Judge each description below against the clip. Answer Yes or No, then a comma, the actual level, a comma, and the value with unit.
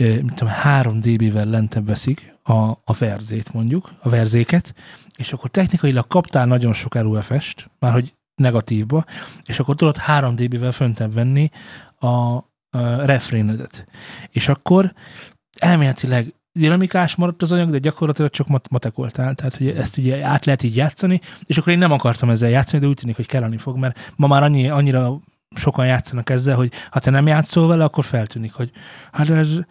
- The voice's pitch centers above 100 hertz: Yes, low, 130 Hz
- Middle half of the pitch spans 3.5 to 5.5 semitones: Yes, average, 4.2 semitones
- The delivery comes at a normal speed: No, fast, 160 wpm